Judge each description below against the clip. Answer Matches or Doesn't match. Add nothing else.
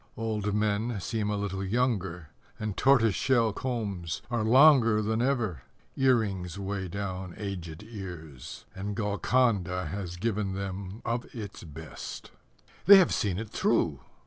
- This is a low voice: Matches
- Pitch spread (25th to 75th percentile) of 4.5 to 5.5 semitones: Doesn't match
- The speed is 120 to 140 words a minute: Matches